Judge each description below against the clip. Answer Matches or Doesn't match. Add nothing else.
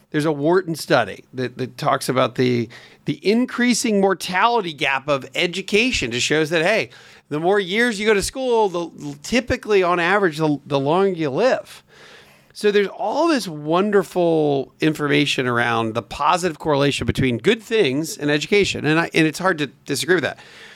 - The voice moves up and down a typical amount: Doesn't match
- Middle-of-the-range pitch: Matches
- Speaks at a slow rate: Doesn't match